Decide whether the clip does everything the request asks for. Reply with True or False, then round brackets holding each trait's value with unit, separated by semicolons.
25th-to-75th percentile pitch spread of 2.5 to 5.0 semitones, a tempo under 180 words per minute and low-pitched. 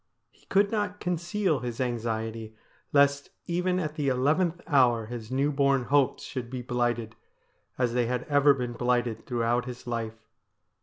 True (3.6 semitones; 155 wpm; 125 Hz)